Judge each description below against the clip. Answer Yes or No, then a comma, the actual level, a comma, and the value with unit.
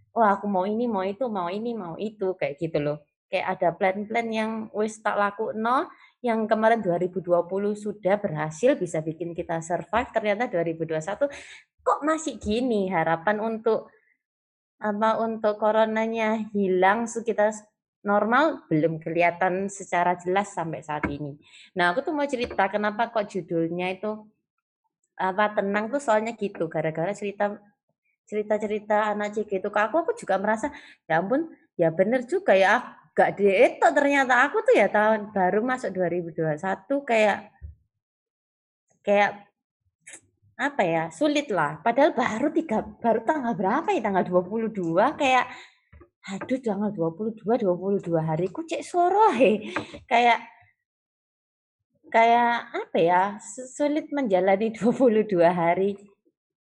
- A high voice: Yes, high, 210 Hz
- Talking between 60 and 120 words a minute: No, average, 130 wpm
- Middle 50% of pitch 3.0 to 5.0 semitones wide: Yes, average, 4.4 semitones